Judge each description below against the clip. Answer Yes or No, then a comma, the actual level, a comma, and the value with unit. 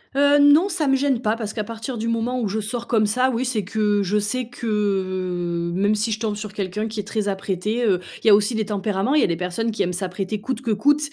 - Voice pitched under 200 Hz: No, high, 215 Hz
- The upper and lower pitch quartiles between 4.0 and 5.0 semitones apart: No, average, 3.2 semitones